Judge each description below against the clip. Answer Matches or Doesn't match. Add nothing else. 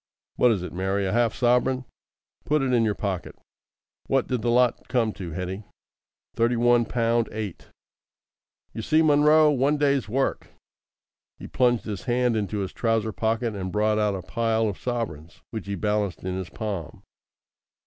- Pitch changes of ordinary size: Matches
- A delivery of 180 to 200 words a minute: Doesn't match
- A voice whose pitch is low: Matches